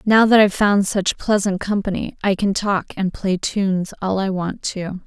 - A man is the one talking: No, female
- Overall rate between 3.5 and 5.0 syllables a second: Yes, 4.7 syllables/s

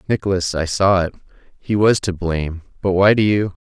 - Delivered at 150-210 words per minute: Yes, average, 200 wpm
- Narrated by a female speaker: No, male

